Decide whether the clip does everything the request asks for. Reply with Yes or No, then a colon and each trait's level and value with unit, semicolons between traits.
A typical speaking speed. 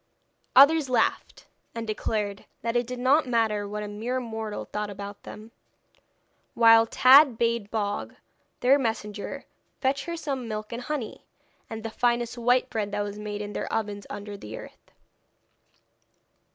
Yes: average, 150 wpm